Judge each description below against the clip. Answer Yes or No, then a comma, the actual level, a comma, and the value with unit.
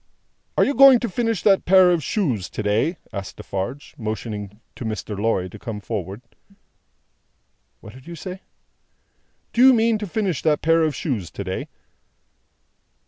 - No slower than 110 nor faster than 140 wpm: No, average, 160 wpm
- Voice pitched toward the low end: No, medium, 145 Hz